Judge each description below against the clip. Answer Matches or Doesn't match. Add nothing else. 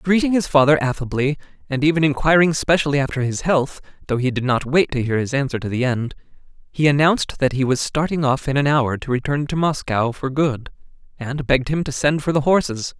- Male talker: Matches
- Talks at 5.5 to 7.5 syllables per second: Matches